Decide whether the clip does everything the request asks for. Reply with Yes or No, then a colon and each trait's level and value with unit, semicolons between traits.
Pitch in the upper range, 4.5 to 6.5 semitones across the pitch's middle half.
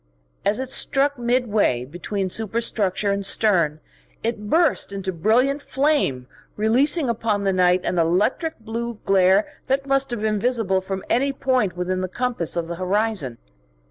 Yes: high, 215 Hz; average, 5.0 semitones